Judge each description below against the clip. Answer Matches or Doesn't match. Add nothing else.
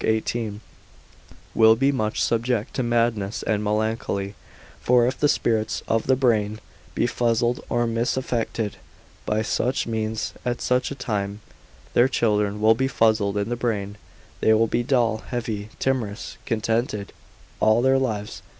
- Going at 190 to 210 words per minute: Doesn't match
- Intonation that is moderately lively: Doesn't match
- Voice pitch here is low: Matches